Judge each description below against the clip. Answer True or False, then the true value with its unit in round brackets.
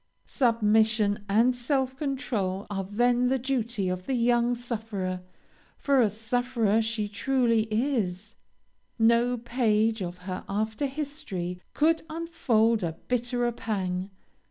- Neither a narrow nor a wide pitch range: True (3.3 semitones)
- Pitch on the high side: True (230 Hz)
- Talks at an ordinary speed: False (120 wpm)